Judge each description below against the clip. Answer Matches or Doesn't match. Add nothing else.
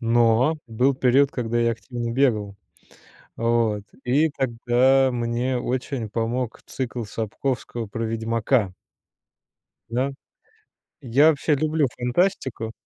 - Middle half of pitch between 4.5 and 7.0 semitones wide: Doesn't match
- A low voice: Matches